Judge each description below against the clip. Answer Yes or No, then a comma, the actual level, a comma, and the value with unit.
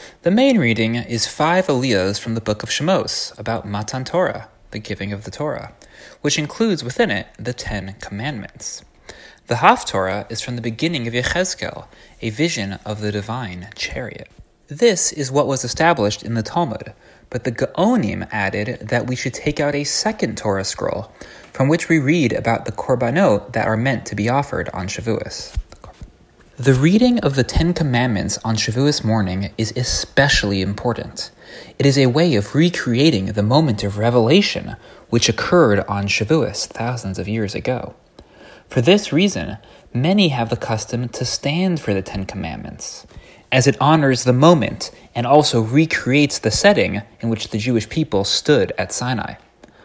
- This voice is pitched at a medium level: No, low, 120 Hz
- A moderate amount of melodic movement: No, wide, 5.9 semitones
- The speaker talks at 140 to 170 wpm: Yes, average, 165 wpm